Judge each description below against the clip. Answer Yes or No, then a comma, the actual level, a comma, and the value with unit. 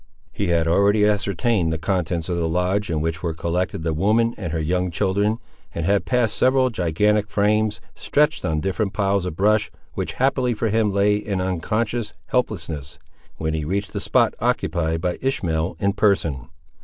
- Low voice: Yes, very low, 95 Hz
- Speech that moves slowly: No, average, 175 wpm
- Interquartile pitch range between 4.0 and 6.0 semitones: Yes, average, 4.3 semitones